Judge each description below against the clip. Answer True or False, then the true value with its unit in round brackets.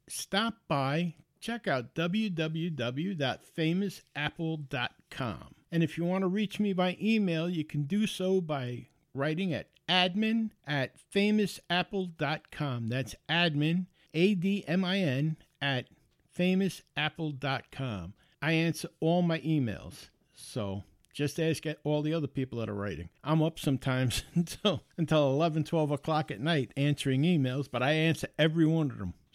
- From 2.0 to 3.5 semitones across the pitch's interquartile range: False (4.1 semitones)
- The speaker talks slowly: True (130 wpm)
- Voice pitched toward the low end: False (155 Hz)